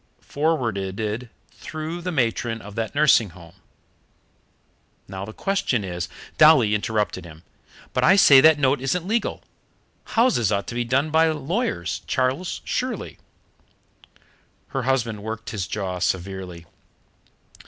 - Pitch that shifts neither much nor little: No, wide, 7.7 semitones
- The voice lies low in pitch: Yes, low, 120 Hz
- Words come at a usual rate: No, slow, 130 wpm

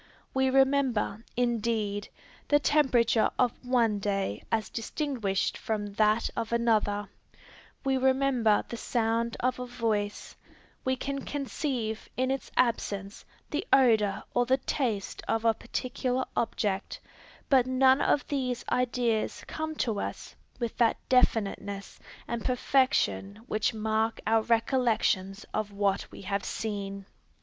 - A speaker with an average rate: No, slow, 125 wpm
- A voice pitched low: No, high, 230 Hz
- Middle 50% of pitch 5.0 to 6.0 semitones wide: No, average, 3.5 semitones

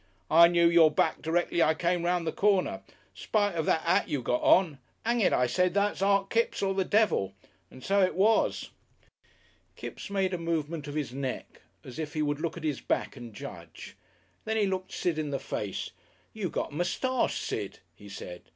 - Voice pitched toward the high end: No, medium, 170 Hz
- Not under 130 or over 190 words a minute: No, average, 200 wpm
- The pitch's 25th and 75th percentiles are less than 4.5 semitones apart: No, average, 4.8 semitones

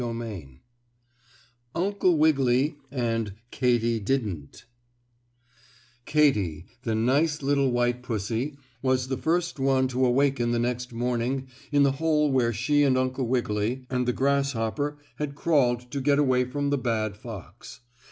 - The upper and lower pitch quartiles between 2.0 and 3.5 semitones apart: Yes, average, 3.2 semitones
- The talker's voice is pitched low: Yes, low, 130 Hz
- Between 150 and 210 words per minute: No, average, 140 wpm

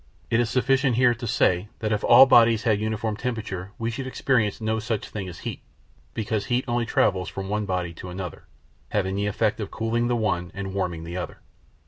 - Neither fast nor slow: No, fast, 210 wpm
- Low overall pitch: Yes, low, 110 Hz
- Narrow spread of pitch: No, average, 3.4 semitones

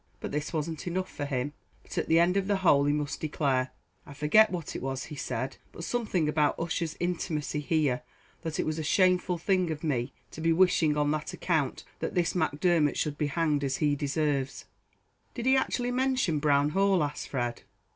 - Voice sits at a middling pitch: Yes, medium, 155 Hz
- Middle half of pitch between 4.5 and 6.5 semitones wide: No, average, 3.6 semitones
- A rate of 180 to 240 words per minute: Yes, average, 200 wpm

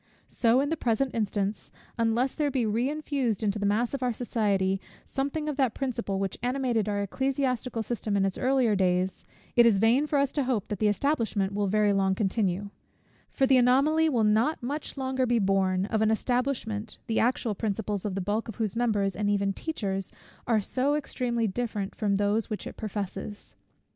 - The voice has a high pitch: Yes, high, 225 Hz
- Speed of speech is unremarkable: Yes, average, 190 wpm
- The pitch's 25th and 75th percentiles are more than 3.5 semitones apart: Yes, average, 4.1 semitones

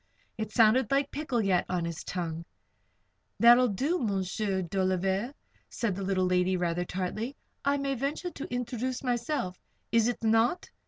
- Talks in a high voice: Yes, high, 220 Hz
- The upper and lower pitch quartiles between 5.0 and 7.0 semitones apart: Yes, average, 5.3 semitones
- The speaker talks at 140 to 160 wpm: Yes, average, 155 wpm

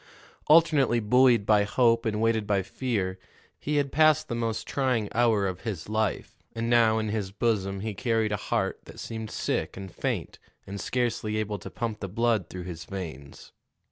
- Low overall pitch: Yes, low, 110 Hz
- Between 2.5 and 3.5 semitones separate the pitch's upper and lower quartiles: Yes, average, 3.1 semitones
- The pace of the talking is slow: No, average, 180 wpm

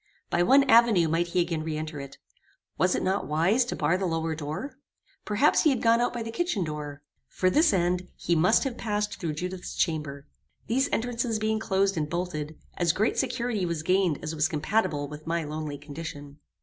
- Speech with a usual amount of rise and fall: No, wide, 6.0 semitones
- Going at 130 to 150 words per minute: No, average, 195 wpm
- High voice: No, medium, 175 Hz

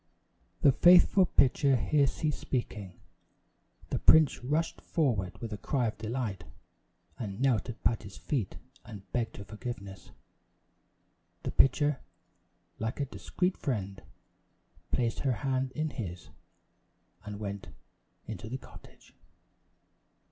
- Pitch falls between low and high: No, low, 120 Hz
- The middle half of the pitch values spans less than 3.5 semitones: No, average, 5.1 semitones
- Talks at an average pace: No, slow, 120 wpm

